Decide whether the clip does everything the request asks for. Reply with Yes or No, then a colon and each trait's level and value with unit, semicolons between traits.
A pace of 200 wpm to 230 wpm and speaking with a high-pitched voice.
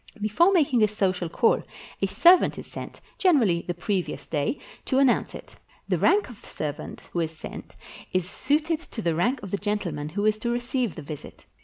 Yes: fast, 205 wpm; high, 210 Hz